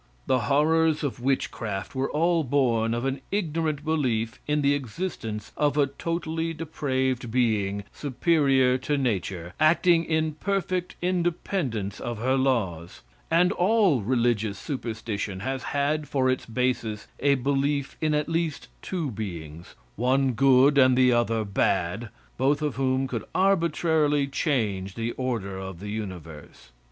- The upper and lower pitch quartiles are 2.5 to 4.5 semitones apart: No, average, 5.3 semitones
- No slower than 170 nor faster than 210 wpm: No, average, 140 wpm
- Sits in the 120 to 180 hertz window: Yes, low, 130 Hz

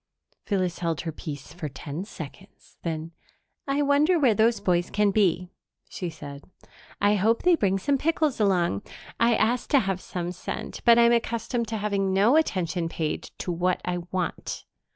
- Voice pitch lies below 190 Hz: No, high, 195 Hz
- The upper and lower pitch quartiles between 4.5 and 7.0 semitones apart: Yes, average, 5.2 semitones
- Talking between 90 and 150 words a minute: No, average, 170 wpm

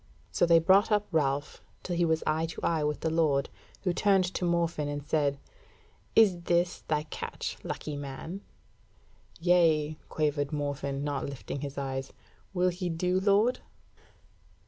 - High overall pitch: No, medium, 160 Hz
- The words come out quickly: No, average, 150 wpm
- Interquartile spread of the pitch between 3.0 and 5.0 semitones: Yes, average, 3.6 semitones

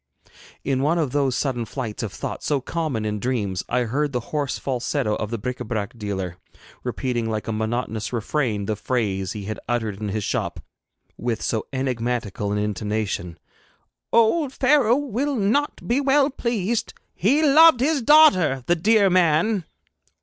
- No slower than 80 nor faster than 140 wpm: No, average, 165 wpm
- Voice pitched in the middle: No, low, 130 Hz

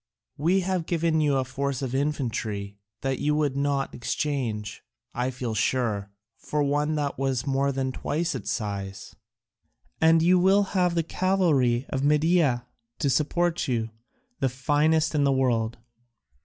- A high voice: No, medium, 140 Hz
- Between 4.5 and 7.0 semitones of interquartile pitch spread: No, average, 4.1 semitones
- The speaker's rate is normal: Yes, average, 150 wpm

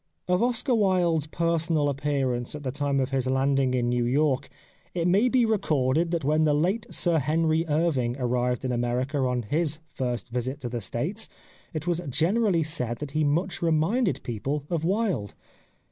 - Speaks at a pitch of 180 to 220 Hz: No, medium, 150 Hz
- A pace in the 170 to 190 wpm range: Yes, average, 180 wpm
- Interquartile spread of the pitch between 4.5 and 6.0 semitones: Yes, average, 4.9 semitones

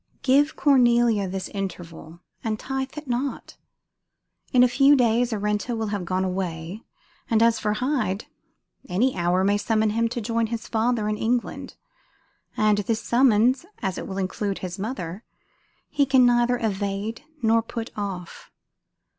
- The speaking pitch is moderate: No, high, 220 Hz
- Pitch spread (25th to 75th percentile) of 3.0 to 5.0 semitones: Yes, average, 3.7 semitones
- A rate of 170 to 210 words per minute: No, average, 150 wpm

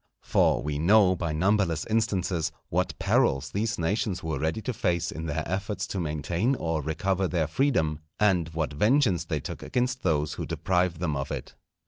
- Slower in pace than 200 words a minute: Yes, average, 175 wpm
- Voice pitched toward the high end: No, very low, 90 Hz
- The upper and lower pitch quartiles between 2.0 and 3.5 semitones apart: No, average, 4.6 semitones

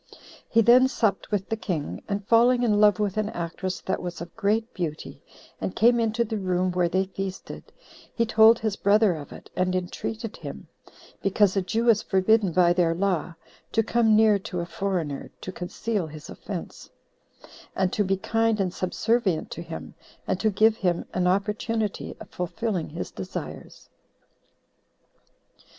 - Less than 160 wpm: No, average, 165 wpm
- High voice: Yes, high, 195 Hz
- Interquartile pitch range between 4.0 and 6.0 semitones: No, average, 3.6 semitones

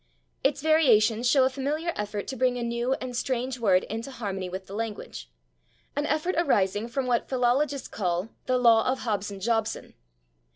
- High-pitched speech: Yes, high, 240 Hz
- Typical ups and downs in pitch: Yes, average, 4.1 semitones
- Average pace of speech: Yes, average, 170 wpm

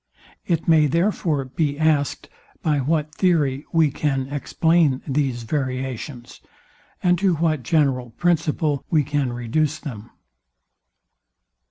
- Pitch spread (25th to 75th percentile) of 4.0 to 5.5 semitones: No, average, 3.3 semitones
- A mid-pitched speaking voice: Yes, medium, 150 Hz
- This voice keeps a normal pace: No, slow, 115 wpm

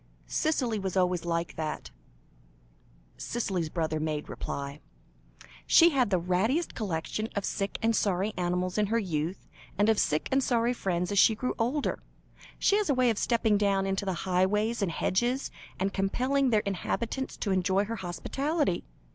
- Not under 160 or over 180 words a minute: Yes, average, 165 wpm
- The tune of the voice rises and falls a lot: No, average, 4.6 semitones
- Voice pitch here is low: No, high, 200 Hz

